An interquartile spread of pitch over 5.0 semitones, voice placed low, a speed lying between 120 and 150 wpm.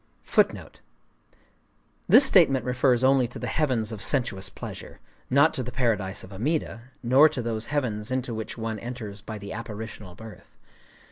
No: average, 3.3 semitones; low, 120 Hz; average, 145 wpm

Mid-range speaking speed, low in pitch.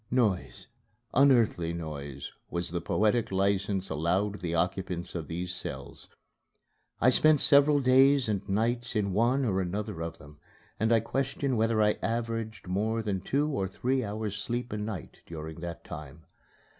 Yes: average, 155 wpm; low, 105 Hz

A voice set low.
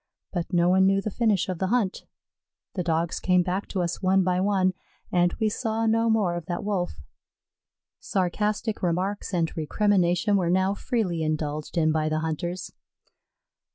No: medium, 185 Hz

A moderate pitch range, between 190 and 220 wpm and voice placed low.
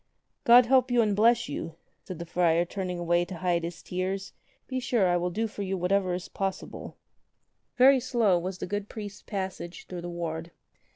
No: average, 3.7 semitones; average, 195 wpm; high, 190 Hz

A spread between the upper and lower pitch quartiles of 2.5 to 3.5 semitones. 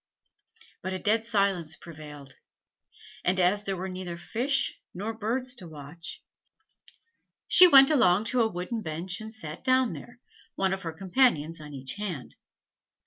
No: average, 5.3 semitones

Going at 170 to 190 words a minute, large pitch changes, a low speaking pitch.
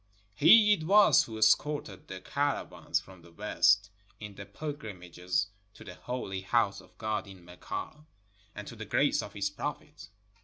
No: average, 160 wpm; wide, 7.2 semitones; low, 105 Hz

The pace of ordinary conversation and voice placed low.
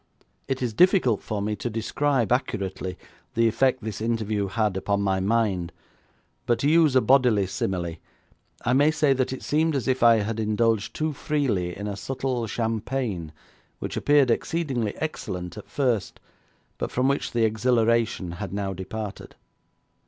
Yes: average, 160 wpm; low, 115 Hz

